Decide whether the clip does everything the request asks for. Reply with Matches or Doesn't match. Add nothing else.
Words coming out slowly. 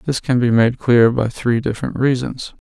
Doesn't match